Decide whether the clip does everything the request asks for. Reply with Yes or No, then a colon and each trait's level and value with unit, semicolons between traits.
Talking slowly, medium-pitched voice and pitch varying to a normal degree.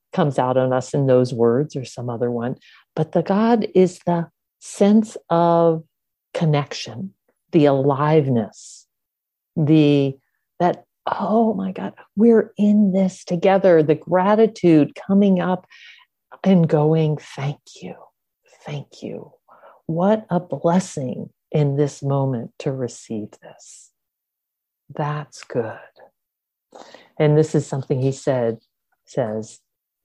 Yes: slow, 115 wpm; medium, 155 Hz; average, 5.0 semitones